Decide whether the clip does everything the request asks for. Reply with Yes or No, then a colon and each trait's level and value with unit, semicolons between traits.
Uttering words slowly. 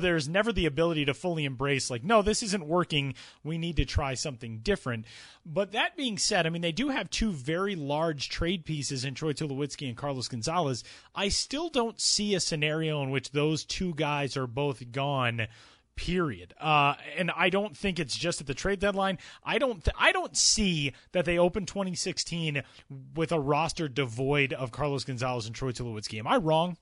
No: average, 195 wpm